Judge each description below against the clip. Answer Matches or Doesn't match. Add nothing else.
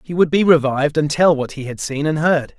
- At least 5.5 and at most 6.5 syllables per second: Matches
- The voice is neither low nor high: Matches